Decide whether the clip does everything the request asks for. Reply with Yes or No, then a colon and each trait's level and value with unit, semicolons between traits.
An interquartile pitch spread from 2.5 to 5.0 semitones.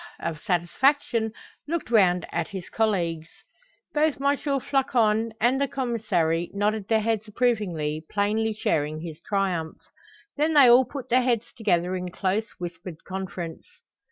No: wide, 5.6 semitones